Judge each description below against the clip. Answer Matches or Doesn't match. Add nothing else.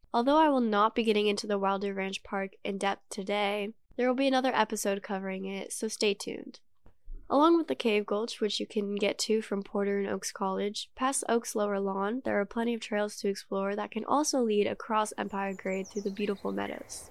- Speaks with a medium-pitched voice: Doesn't match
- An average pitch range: Doesn't match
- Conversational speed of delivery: Doesn't match